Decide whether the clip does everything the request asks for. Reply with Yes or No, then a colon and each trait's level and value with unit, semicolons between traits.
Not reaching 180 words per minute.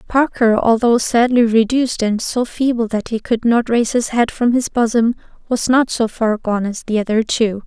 No: fast, 205 wpm